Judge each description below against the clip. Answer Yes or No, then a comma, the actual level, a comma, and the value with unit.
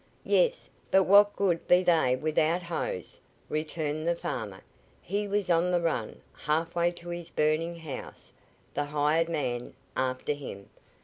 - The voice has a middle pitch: Yes, medium, 165 Hz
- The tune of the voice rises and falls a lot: No, average, 3.0 semitones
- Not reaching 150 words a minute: Yes, average, 140 wpm